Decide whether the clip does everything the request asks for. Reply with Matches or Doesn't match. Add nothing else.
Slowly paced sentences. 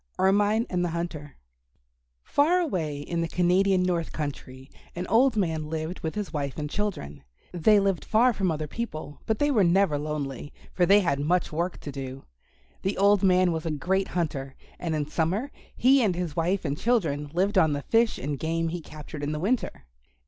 Doesn't match